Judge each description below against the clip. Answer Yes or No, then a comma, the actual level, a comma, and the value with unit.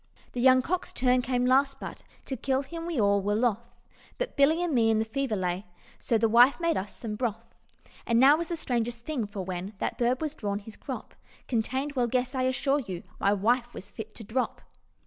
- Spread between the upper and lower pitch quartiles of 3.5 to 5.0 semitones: Yes, average, 3.8 semitones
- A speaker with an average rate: No, fast, 220 wpm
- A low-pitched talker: No, high, 245 Hz